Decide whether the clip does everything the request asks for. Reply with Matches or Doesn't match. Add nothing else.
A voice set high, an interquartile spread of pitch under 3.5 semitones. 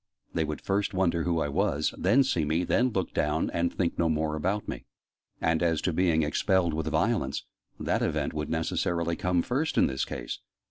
Doesn't match